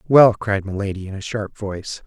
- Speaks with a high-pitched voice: No, low, 105 Hz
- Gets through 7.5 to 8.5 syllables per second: No, 5.3 syllables/s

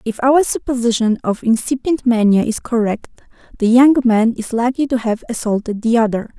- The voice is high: Yes, high, 235 Hz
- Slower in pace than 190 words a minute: Yes, average, 170 wpm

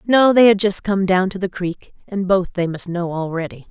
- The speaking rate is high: Yes, fast, 245 wpm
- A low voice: No, high, 190 Hz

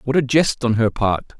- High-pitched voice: No, low, 125 Hz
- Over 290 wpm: No, fast, 260 wpm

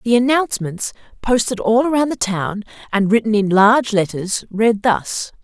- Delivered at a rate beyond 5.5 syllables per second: No, 4.8 syllables/s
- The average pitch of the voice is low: No, high, 220 Hz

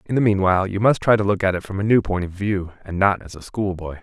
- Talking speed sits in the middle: No, fast, 315 wpm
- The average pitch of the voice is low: Yes, very low, 95 Hz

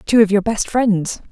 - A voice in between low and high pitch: No, high, 210 Hz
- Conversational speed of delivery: No, fast, 230 wpm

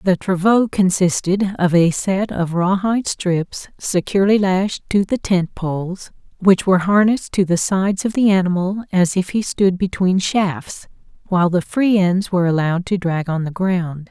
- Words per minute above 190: No, average, 175 wpm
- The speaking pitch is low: No, medium, 185 Hz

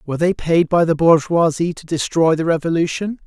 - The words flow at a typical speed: Yes, average, 185 wpm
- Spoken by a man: Yes, male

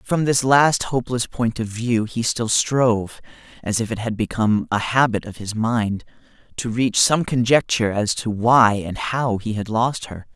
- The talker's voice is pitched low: Yes, low, 115 Hz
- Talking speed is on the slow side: No, average, 190 wpm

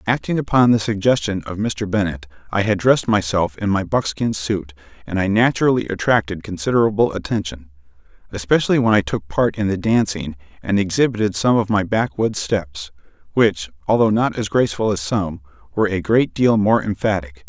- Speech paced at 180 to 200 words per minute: No, average, 170 wpm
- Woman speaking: No, male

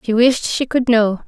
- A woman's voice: Yes, female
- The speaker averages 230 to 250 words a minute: Yes, fast, 235 wpm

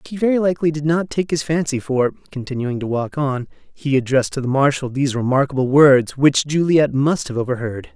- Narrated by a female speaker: No, male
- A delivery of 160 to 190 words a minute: No, fast, 205 wpm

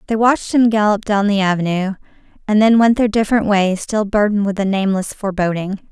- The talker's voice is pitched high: Yes, high, 205 Hz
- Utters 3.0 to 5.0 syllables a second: No, 6.1 syllables/s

